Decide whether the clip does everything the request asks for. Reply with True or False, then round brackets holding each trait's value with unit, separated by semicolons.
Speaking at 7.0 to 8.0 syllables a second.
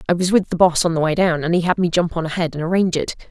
True (7.3 syllables/s)